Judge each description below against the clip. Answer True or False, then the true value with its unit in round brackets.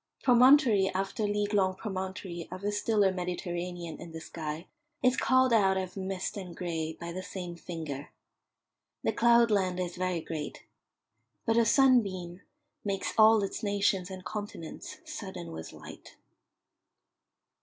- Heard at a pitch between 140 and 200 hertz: True (190 Hz)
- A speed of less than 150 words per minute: True (135 wpm)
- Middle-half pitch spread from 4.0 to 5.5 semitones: False (3.1 semitones)